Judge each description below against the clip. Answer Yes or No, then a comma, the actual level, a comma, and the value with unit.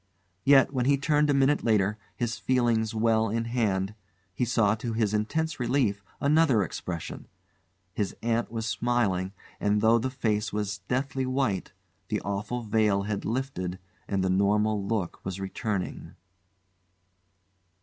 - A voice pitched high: No, low, 110 Hz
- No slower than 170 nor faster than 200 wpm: No, average, 140 wpm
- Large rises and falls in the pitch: No, average, 3.7 semitones